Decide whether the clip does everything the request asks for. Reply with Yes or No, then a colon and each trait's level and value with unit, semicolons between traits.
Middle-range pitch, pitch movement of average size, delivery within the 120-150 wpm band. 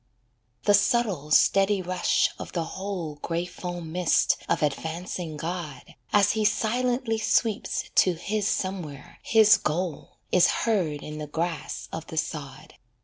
Yes: medium, 180 Hz; average, 4.4 semitones; average, 140 wpm